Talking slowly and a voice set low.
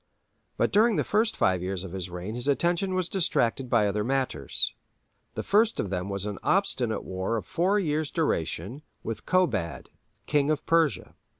No: average, 175 wpm; low, 130 Hz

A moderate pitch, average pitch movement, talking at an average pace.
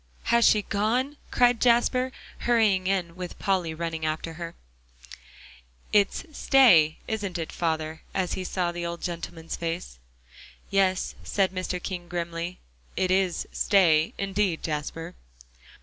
No: medium, 180 Hz; average, 3.1 semitones; slow, 125 wpm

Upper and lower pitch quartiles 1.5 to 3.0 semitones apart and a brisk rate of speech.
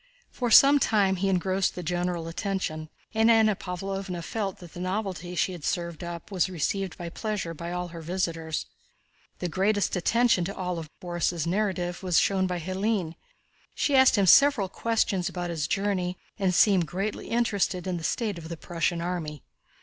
No: narrow, 2.6 semitones; average, 175 wpm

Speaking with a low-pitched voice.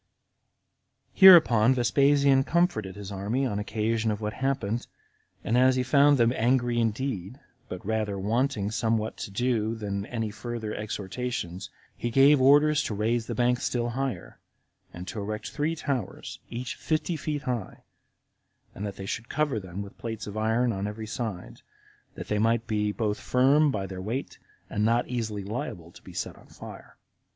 Yes: low, 115 Hz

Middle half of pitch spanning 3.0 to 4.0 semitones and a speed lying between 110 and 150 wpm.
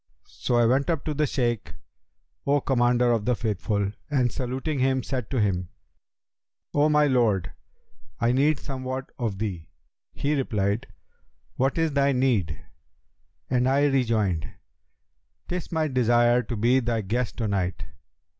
Yes: average, 3.7 semitones; average, 145 wpm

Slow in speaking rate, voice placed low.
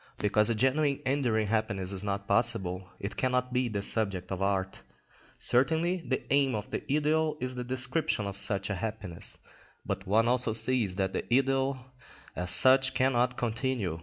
No: average, 165 wpm; low, 115 Hz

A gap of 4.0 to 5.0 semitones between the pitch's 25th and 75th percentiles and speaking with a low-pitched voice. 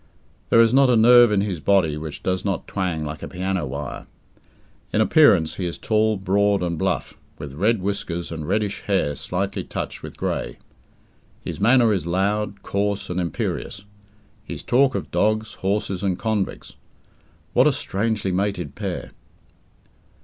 No: average, 3.3 semitones; low, 100 Hz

